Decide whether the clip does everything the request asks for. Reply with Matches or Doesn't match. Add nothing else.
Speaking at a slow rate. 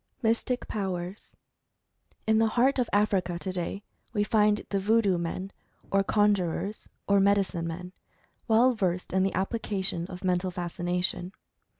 Matches